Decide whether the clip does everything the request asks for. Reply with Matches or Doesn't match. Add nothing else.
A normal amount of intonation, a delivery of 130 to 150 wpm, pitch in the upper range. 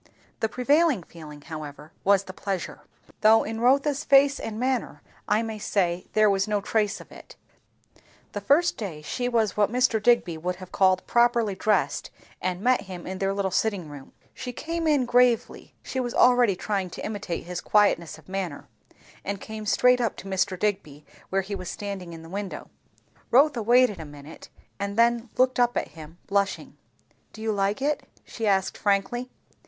Doesn't match